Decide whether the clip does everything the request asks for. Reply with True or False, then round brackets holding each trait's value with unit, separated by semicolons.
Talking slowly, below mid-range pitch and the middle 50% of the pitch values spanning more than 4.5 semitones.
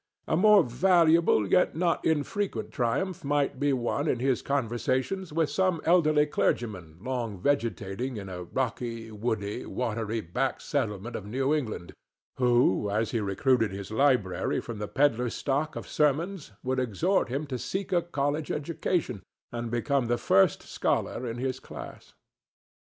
False (150 wpm; 130 Hz; 5.0 semitones)